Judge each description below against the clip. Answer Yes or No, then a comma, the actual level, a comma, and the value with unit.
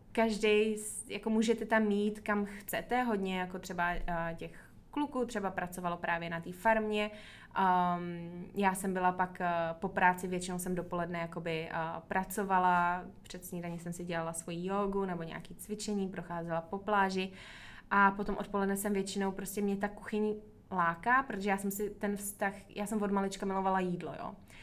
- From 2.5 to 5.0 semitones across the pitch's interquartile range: Yes, average, 2.8 semitones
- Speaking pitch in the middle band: No, high, 195 Hz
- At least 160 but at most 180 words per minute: Yes, fast, 170 wpm